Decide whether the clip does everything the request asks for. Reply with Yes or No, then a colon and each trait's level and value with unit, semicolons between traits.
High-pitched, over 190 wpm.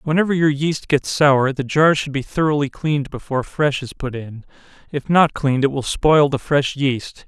No: medium, 140 Hz; average, 200 wpm